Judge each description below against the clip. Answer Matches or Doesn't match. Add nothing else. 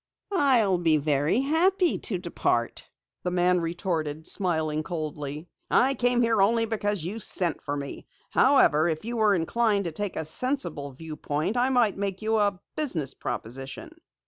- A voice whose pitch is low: Doesn't match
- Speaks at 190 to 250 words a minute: Doesn't match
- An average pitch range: Doesn't match